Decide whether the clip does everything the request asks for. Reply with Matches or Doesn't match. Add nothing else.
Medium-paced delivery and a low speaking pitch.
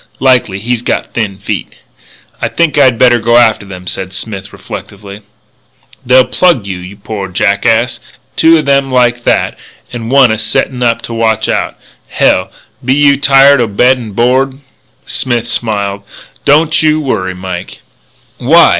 Matches